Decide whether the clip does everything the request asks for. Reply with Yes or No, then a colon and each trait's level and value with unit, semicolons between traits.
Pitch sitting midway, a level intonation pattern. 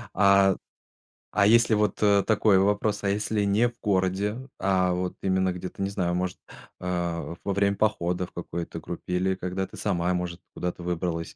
No: very low, 95 Hz; narrow, 2.2 semitones